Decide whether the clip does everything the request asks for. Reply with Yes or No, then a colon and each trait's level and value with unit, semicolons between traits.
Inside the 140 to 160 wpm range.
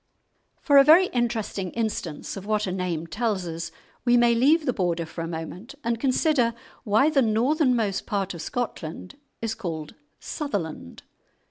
Yes: average, 155 wpm